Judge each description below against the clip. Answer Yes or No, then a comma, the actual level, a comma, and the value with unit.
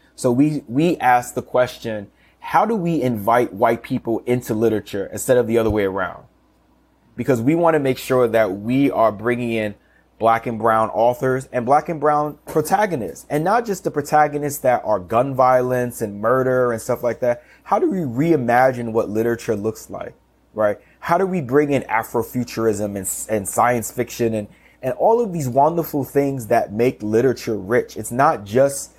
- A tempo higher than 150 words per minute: Yes, average, 180 wpm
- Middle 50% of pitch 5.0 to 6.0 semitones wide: No, average, 3.7 semitones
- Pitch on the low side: Yes, low, 125 Hz